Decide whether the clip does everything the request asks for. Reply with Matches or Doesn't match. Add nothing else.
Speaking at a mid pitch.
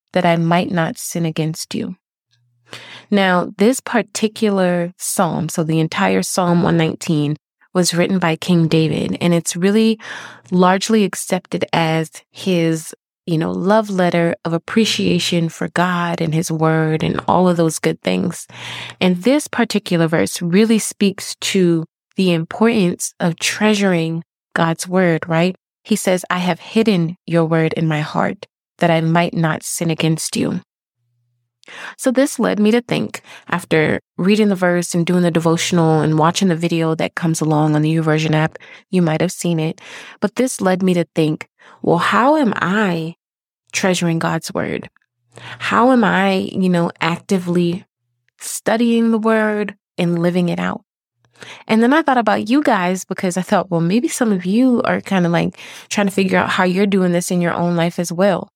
Matches